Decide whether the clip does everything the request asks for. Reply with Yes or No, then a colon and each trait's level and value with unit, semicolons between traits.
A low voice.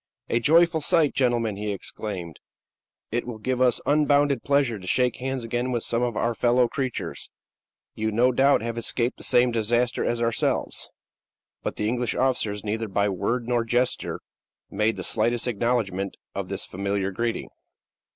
Yes: low, 120 Hz